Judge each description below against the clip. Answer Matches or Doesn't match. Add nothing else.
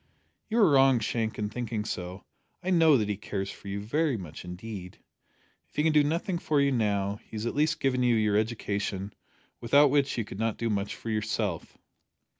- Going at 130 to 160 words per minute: Doesn't match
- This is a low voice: Matches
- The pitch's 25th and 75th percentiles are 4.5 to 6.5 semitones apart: Matches